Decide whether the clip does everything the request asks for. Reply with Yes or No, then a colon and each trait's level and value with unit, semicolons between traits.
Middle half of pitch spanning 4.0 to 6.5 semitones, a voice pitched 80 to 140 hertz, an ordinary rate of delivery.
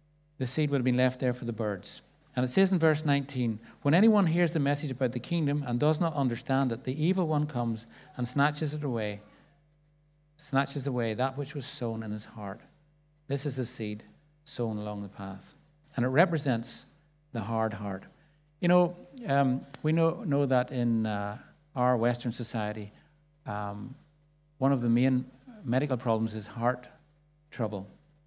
Yes: average, 4.3 semitones; low, 135 Hz; average, 175 wpm